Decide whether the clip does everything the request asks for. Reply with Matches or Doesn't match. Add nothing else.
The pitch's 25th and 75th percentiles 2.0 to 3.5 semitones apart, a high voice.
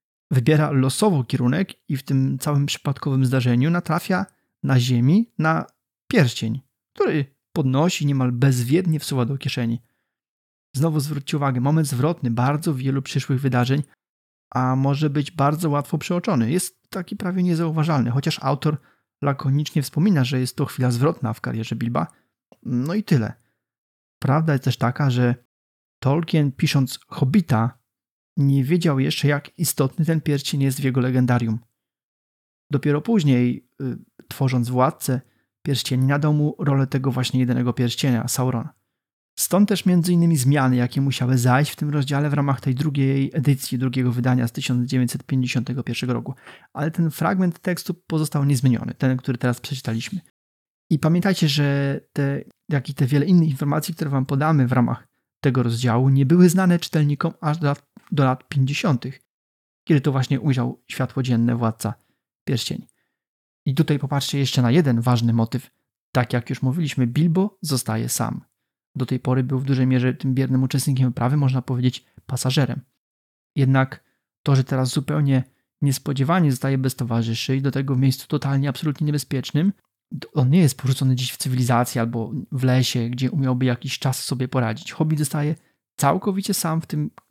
Doesn't match